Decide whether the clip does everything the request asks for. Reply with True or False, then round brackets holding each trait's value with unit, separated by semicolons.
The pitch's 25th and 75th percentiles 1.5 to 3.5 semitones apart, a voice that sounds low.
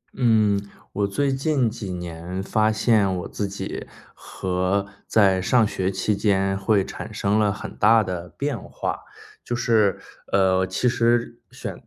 True (3.0 semitones; 100 Hz)